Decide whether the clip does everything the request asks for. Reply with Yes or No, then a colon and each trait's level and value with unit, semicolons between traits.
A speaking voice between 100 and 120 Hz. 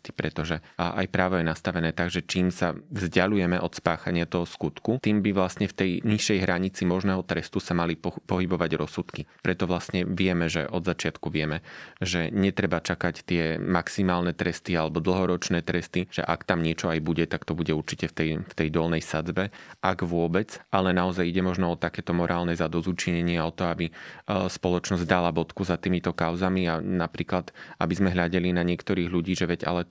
No: very low, 90 Hz